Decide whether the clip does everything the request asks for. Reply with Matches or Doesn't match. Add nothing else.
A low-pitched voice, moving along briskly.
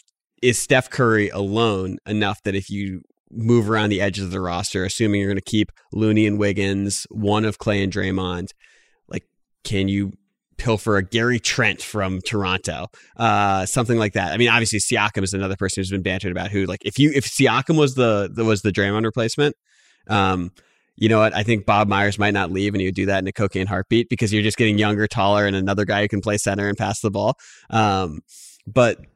Matches